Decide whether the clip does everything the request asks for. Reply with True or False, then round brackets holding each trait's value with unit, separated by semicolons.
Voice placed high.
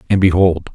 False (90 Hz)